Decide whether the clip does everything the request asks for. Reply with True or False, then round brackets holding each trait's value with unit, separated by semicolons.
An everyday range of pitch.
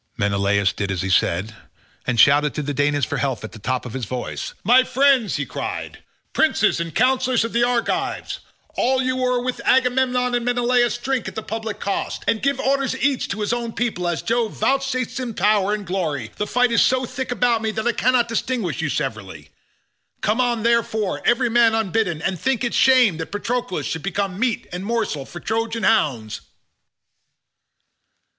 False (7.5 semitones)